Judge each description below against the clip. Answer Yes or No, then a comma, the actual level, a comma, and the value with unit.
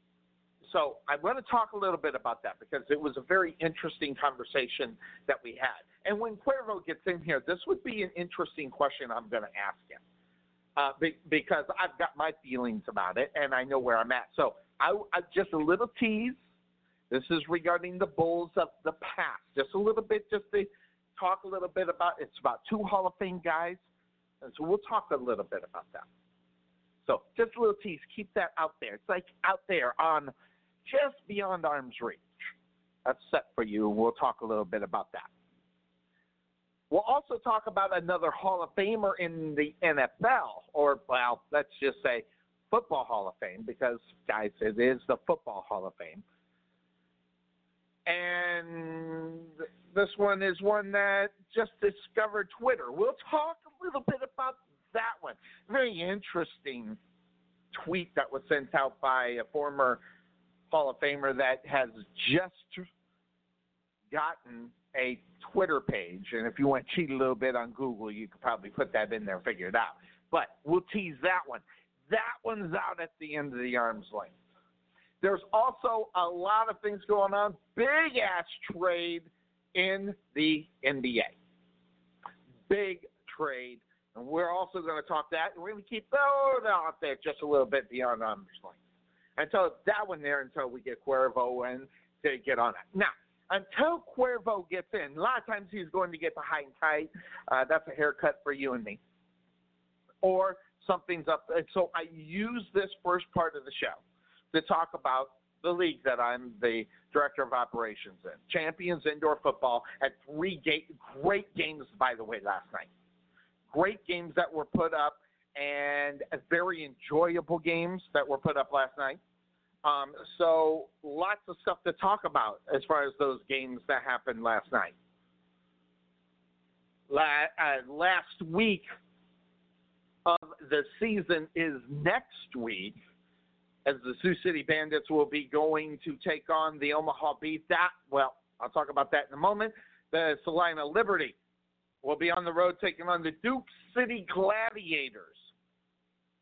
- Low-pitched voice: No, medium, 155 Hz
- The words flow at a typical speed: Yes, average, 170 wpm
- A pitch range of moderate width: No, wide, 7.6 semitones